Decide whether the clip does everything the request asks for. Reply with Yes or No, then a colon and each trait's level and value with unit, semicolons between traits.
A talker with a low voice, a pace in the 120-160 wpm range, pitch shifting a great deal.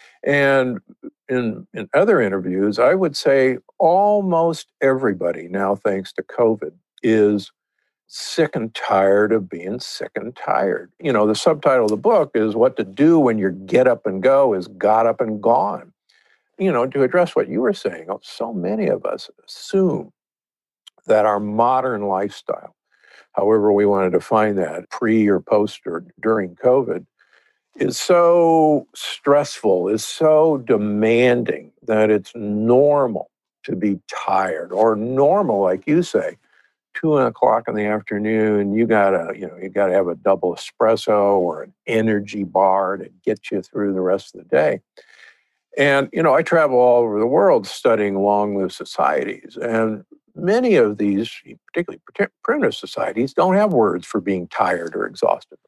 Yes: low, 110 Hz; average, 155 wpm; wide, 5.8 semitones